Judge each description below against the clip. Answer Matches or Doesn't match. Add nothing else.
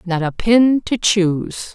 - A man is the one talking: Doesn't match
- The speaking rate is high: Doesn't match